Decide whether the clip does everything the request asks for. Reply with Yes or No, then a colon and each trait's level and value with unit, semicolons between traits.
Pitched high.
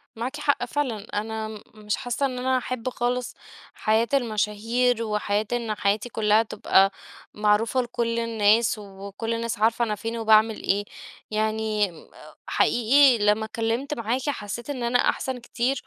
Yes: high, 225 Hz